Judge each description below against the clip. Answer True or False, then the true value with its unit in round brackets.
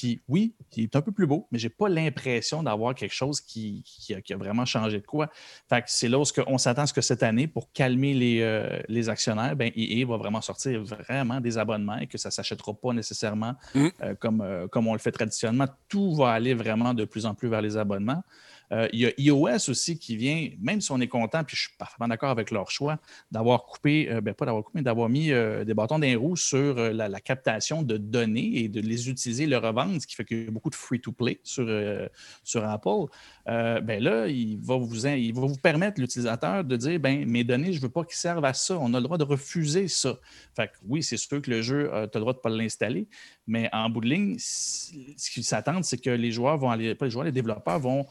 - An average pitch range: True (3.8 semitones)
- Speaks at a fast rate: True (260 wpm)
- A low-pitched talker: True (120 Hz)